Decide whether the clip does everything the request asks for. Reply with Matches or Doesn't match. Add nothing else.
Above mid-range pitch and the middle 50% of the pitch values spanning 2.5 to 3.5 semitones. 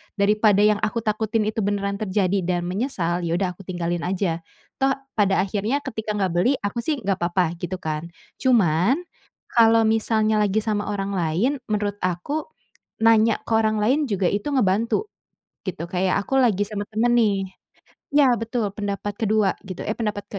Matches